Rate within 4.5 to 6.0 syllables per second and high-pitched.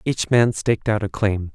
No: 4.9 syllables/s; low, 105 Hz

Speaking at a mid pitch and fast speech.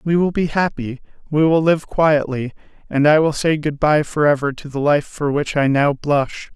Yes: medium, 150 Hz; fast, 210 wpm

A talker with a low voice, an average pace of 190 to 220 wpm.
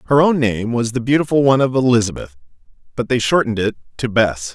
Yes: low, 120 Hz; average, 200 wpm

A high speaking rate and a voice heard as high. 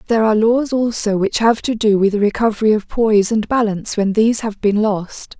Yes: fast, 225 wpm; high, 215 Hz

